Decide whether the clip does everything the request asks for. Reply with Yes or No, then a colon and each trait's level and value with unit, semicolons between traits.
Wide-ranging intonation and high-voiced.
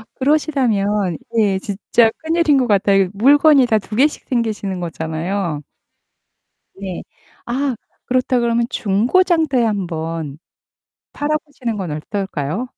Yes: wide, 5.7 semitones; high, 220 Hz